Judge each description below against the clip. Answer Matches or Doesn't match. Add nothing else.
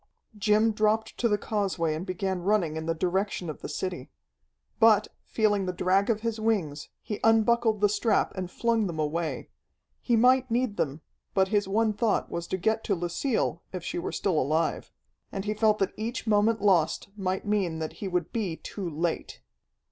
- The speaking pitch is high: Matches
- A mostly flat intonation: Doesn't match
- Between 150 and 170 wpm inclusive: Doesn't match